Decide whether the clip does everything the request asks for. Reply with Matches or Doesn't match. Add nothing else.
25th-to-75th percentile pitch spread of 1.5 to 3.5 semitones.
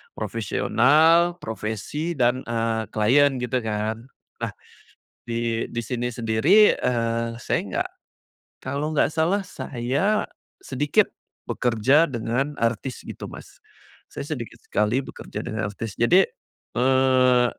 Doesn't match